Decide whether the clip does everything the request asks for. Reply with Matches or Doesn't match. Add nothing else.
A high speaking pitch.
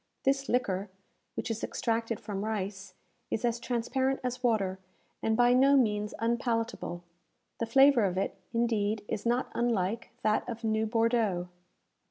Matches